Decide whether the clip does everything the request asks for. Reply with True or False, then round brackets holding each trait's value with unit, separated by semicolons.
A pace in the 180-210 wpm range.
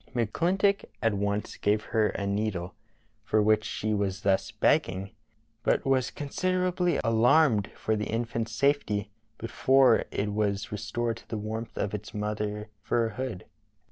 False (150 wpm)